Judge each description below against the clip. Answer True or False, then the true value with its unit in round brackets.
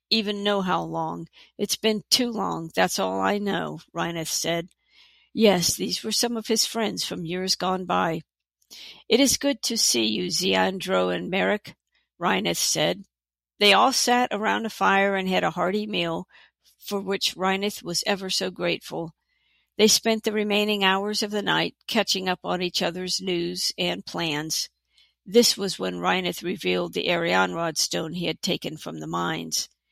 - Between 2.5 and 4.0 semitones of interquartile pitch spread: False (4.5 semitones)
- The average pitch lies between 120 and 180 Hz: False (190 Hz)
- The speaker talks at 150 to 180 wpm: True (170 wpm)